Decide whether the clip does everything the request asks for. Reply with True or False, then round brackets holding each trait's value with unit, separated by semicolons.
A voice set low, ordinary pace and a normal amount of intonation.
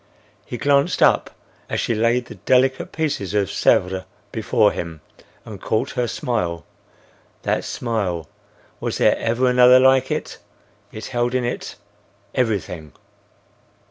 False (120 Hz; 120 wpm; 4.7 semitones)